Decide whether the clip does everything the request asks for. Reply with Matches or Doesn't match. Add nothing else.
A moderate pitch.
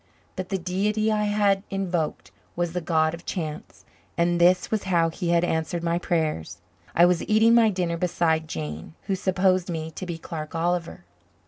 Matches